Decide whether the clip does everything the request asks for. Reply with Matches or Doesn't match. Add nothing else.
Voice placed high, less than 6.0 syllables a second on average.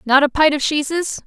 Matches